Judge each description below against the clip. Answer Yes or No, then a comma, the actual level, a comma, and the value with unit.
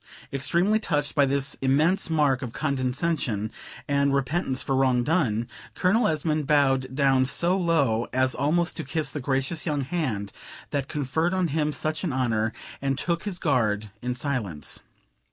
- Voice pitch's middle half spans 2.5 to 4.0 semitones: Yes, average, 3.7 semitones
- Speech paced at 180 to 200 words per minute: No, average, 155 wpm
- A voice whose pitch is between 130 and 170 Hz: Yes, medium, 140 Hz